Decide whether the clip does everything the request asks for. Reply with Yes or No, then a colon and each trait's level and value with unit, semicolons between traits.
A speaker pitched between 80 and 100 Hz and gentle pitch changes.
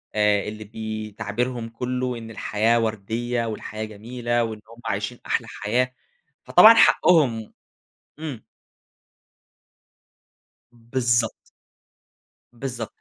No: low, 115 Hz; narrow, 2.2 semitones